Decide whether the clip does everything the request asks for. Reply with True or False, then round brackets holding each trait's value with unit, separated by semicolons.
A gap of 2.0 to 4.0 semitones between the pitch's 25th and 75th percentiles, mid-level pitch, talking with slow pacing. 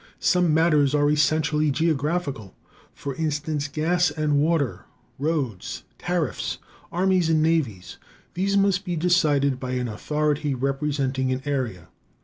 True (3.2 semitones; 150 Hz; 125 wpm)